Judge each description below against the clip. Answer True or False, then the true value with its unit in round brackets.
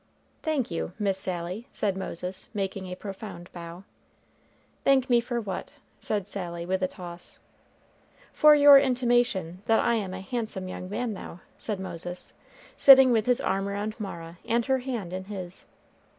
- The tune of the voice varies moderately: True (4.5 semitones)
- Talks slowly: False (160 wpm)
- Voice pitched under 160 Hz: False (195 Hz)